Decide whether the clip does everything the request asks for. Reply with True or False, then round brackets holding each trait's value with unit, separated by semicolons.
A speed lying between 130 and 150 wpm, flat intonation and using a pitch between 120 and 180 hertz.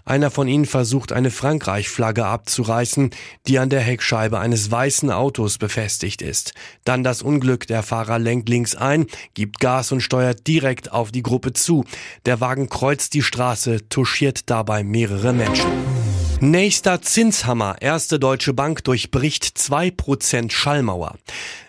False (140 wpm; 3.1 semitones; 125 Hz)